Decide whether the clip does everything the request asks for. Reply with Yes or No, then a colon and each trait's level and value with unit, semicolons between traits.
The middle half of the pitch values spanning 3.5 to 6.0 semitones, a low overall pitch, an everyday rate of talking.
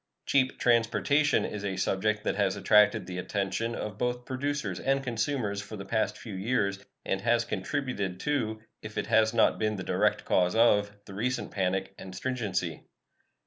Yes: average, 3.9 semitones; low, 110 Hz; average, 170 wpm